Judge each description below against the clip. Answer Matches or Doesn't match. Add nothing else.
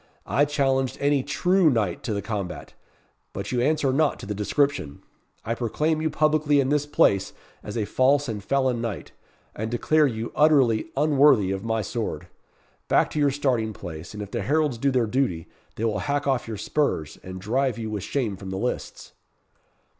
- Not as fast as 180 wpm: Doesn't match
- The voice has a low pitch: Matches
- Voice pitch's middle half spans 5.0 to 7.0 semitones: Matches